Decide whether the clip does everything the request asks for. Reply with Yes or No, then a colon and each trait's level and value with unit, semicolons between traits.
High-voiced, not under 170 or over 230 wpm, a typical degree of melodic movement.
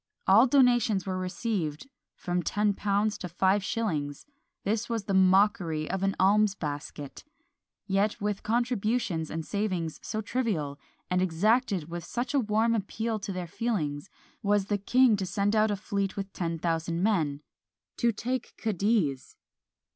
No: high, 200 Hz; average, 150 wpm; average, 4.0 semitones